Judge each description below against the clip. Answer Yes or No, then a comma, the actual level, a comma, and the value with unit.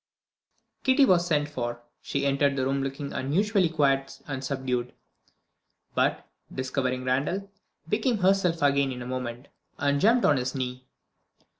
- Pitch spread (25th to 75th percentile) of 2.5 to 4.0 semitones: No, average, 4.7 semitones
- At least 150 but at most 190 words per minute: No, average, 140 wpm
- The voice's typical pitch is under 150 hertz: Yes, medium, 140 Hz